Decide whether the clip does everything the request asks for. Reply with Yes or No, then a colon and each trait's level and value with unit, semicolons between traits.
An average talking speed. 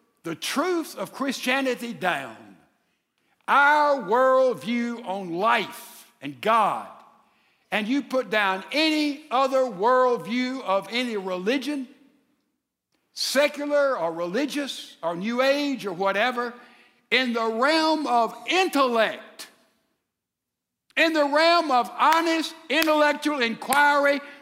No: slow, 100 wpm